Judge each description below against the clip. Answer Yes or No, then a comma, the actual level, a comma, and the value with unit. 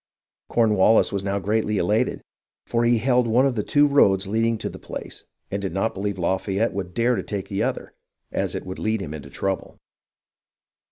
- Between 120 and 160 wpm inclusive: No, average, 190 wpm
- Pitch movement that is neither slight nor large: Yes, average, 3.1 semitones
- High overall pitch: No, low, 105 Hz